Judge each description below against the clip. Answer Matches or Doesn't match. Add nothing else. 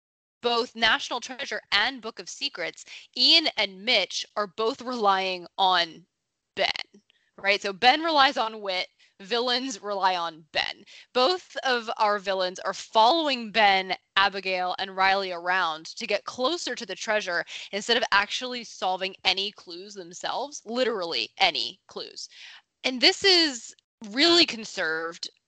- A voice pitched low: Doesn't match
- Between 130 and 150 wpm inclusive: Matches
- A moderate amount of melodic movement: Matches